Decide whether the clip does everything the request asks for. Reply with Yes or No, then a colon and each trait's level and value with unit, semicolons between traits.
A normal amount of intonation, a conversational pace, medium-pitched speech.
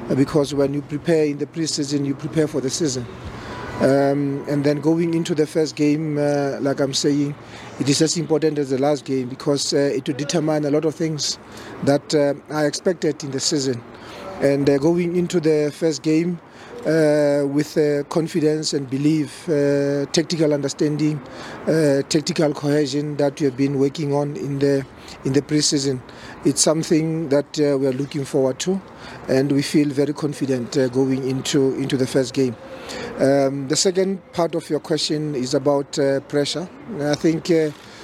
No: narrow, 2.0 semitones; average, 180 wpm; medium, 145 Hz